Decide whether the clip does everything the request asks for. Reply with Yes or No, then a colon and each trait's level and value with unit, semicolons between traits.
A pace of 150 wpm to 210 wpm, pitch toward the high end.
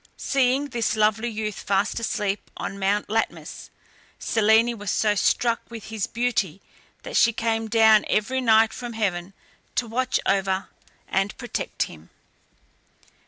No: slow, 135 wpm; high, 220 Hz